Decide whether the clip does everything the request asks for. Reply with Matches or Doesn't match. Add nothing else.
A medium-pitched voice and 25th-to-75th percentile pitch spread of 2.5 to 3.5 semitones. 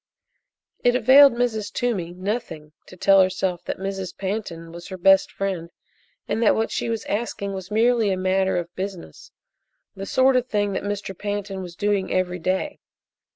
Doesn't match